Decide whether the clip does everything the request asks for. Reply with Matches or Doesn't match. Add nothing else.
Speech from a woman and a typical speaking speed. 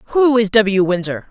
Matches